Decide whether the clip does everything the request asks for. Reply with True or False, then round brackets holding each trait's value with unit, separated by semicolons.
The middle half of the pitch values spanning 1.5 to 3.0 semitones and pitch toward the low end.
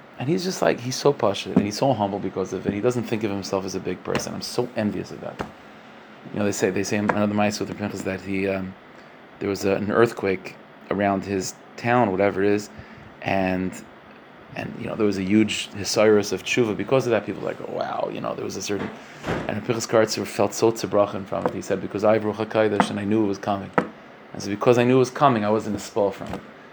True (2.5 semitones; 105 Hz)